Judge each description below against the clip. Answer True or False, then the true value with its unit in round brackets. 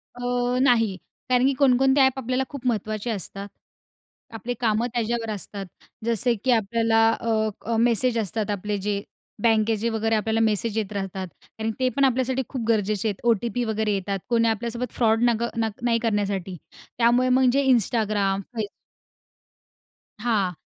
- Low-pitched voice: False (225 Hz)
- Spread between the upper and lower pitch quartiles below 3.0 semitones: True (2.6 semitones)